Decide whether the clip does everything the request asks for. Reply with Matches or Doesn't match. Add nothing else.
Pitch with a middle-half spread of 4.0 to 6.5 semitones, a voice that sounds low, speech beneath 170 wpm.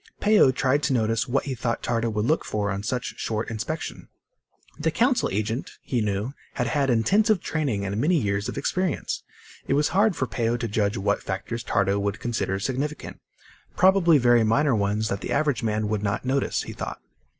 Doesn't match